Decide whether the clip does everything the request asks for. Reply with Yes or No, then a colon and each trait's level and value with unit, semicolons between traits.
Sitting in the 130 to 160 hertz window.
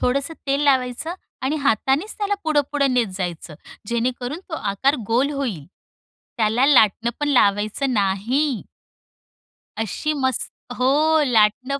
No: very high, 255 Hz